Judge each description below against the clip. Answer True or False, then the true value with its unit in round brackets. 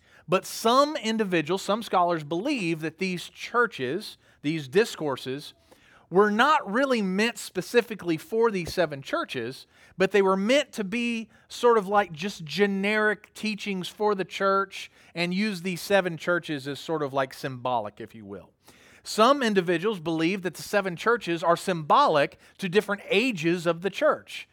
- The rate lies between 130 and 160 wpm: True (155 wpm)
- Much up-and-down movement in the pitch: False (4.4 semitones)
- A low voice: False (190 Hz)